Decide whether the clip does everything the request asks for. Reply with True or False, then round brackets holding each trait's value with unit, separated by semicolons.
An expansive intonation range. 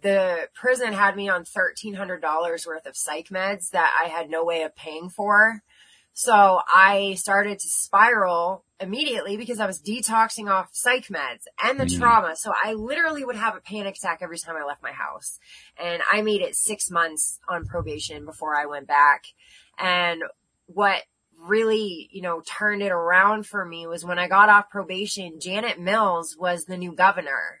False (3.7 semitones)